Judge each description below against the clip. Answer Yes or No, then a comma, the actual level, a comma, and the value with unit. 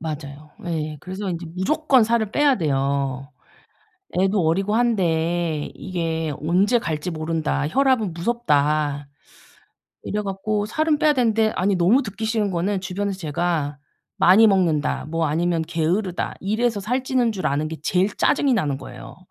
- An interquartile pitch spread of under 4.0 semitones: No, wide, 5.4 semitones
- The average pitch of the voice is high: No, medium, 180 Hz